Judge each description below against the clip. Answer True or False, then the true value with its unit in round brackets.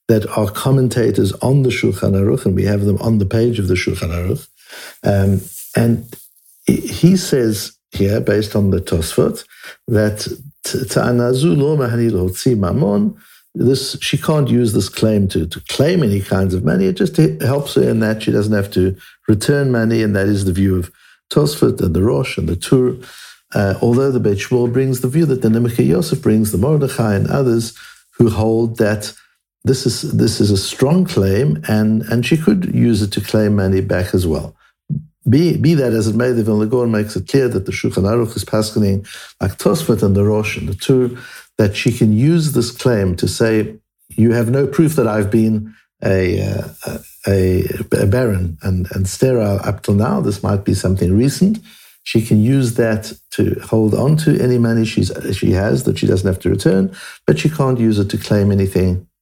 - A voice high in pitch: False (110 Hz)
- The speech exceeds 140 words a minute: True (190 wpm)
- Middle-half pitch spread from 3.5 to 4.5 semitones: True (4.2 semitones)